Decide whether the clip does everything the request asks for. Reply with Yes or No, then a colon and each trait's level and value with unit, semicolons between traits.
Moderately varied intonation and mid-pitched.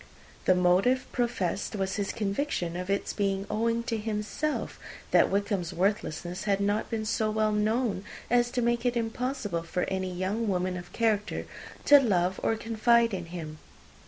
No: average, 3.8 semitones; high, 210 Hz